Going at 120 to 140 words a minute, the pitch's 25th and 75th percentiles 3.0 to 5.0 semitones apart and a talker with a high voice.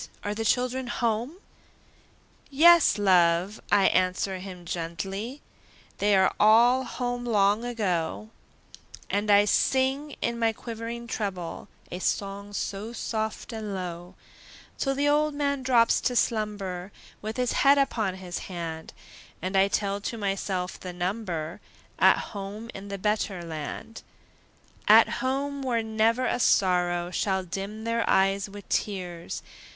Yes: slow, 135 wpm; average, 4.0 semitones; high, 205 Hz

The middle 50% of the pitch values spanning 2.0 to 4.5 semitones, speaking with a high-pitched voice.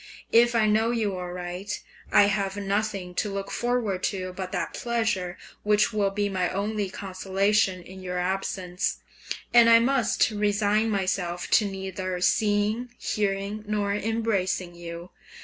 Yes: narrow, 2.4 semitones; high, 200 Hz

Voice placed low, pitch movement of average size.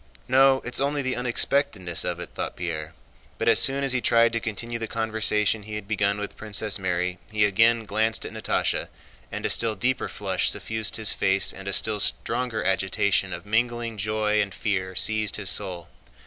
Yes: low, 105 Hz; average, 3.2 semitones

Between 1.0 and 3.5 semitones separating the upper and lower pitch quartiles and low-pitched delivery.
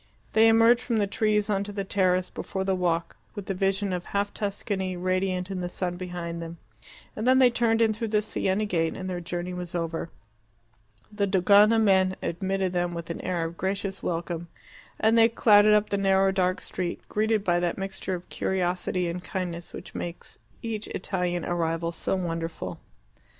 No: average, 2.7 semitones; high, 190 Hz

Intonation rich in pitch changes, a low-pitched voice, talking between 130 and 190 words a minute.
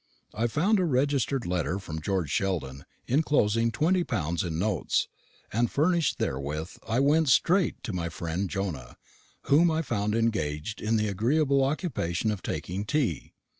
Yes: wide, 8.3 semitones; low, 110 Hz; average, 150 wpm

